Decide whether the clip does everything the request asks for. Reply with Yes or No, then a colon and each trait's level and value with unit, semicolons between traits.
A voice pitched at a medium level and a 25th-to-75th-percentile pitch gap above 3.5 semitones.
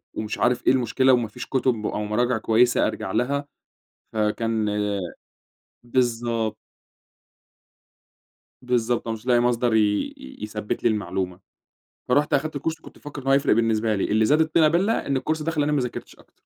No: low, 120 Hz; average, 4.0 semitones